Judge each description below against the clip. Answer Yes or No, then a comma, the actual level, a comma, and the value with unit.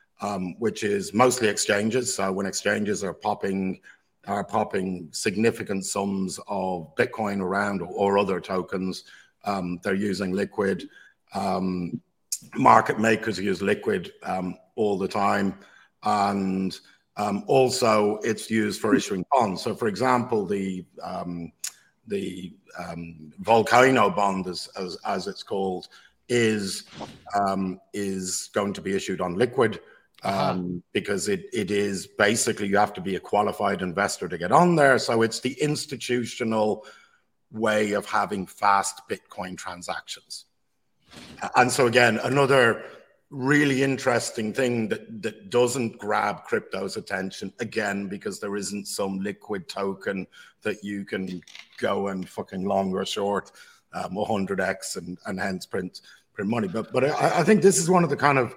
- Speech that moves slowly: No, average, 145 wpm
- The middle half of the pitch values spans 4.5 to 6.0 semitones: No, average, 3.1 semitones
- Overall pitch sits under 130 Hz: Yes, low, 100 Hz